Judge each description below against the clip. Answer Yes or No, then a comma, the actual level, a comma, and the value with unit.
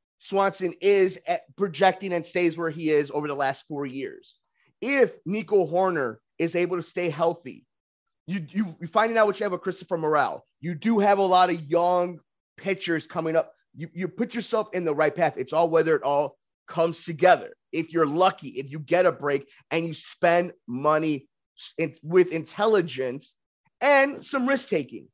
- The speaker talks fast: No, average, 185 wpm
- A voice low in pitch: No, medium, 175 Hz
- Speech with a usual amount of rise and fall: Yes, average, 3.6 semitones